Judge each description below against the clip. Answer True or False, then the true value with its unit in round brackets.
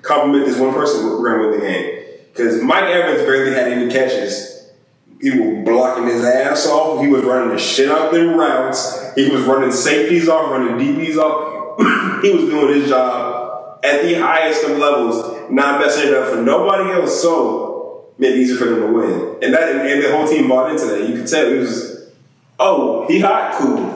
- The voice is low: False (145 Hz)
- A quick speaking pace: True (210 wpm)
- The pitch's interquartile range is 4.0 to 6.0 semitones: True (4.6 semitones)